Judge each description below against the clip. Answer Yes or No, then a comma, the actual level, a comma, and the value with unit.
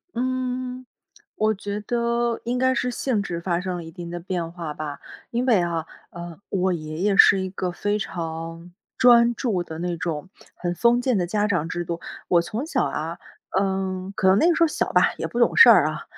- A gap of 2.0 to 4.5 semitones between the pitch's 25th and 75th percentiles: No, wide, 5.6 semitones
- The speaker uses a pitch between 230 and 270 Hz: No, high, 190 Hz